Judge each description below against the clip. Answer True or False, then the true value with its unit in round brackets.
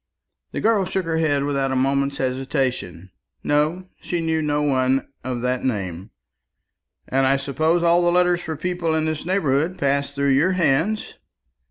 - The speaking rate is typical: True (165 wpm)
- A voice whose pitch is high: False (145 Hz)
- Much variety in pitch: False (4.1 semitones)